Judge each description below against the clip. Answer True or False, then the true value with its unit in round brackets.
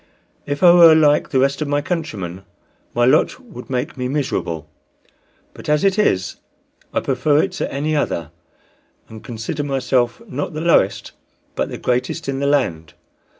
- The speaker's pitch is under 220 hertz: True (140 Hz)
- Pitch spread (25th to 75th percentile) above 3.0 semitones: True (4.0 semitones)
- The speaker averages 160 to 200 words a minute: True (165 wpm)